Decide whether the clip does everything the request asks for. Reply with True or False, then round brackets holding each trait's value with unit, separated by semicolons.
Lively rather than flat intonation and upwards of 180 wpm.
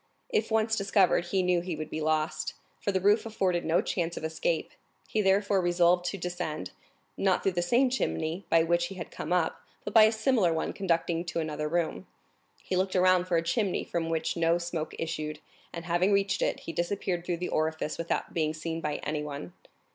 False (2.8 semitones; 200 wpm)